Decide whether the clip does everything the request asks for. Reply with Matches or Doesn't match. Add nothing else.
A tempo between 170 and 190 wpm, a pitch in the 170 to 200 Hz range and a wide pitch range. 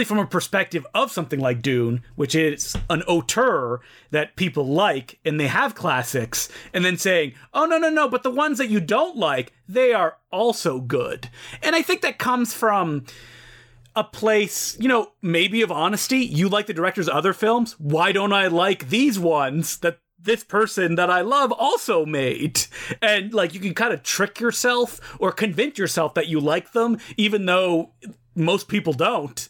Matches